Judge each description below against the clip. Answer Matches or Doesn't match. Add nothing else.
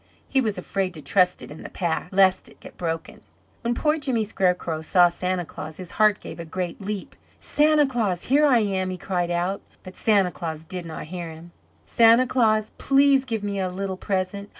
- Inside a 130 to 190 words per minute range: Doesn't match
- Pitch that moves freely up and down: Doesn't match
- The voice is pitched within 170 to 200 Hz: Matches